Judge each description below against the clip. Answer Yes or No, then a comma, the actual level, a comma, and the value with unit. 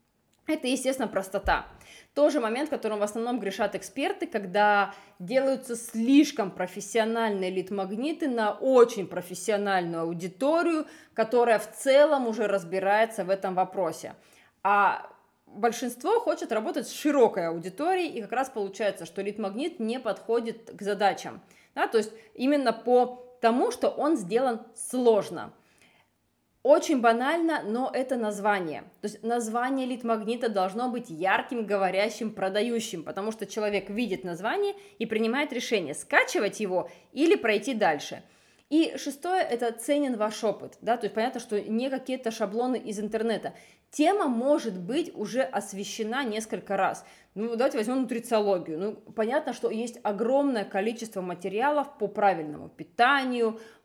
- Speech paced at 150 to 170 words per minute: No, average, 135 wpm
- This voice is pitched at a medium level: No, high, 225 Hz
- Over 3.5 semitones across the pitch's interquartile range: Yes, average, 4.2 semitones